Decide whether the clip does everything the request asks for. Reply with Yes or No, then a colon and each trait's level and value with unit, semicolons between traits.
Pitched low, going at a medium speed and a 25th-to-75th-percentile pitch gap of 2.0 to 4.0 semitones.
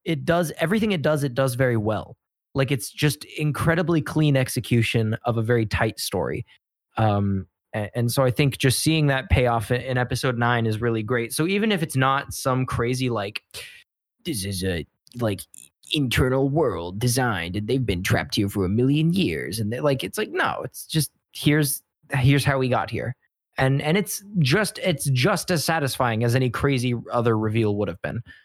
No: low, 130 Hz; average, 190 wpm; average, 4.6 semitones